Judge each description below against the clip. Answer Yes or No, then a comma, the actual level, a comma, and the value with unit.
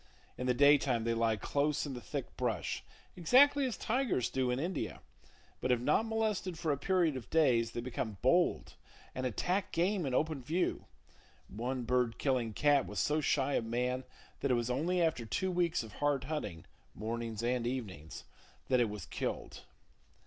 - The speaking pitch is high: No, low, 130 Hz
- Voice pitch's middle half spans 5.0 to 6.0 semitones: Yes, wide, 5.6 semitones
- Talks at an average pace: Yes, average, 180 wpm